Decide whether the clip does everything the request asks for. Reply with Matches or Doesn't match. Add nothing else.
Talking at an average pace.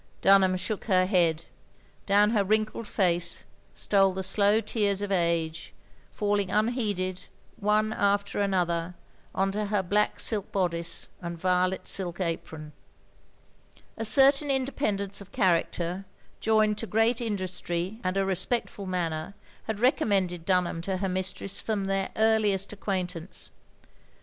Doesn't match